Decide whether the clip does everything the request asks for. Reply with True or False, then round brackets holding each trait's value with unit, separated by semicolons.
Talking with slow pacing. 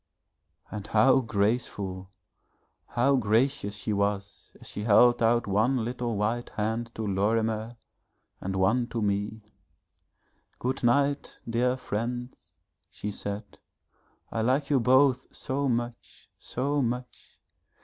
True (120 wpm)